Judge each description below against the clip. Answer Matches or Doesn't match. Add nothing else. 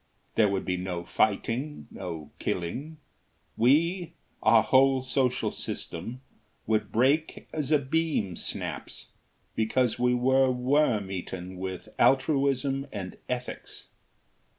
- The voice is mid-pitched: Doesn't match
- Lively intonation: Matches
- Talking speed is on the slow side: Matches